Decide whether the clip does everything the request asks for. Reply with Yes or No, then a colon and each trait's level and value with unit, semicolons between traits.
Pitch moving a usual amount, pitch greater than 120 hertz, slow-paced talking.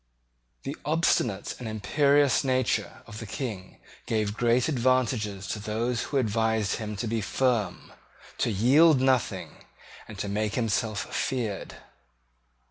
No: average, 3.4 semitones; low, 115 Hz; slow, 130 wpm